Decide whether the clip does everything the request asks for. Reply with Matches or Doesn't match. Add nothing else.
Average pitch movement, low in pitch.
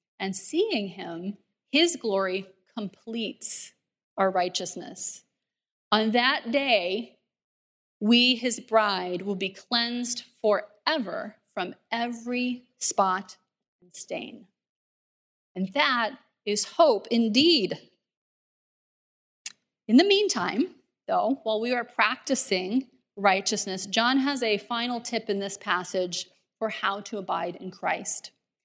Doesn't match